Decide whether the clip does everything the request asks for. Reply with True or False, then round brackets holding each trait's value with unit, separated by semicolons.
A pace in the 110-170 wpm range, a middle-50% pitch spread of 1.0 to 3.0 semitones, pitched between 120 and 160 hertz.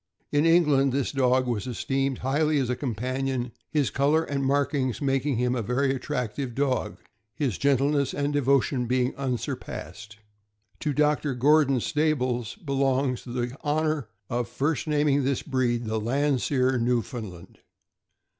True (135 wpm; 2.6 semitones; 135 Hz)